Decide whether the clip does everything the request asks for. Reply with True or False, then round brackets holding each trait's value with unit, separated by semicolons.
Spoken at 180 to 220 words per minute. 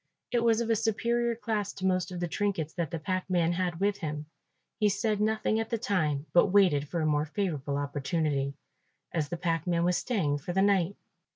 True (200 wpm)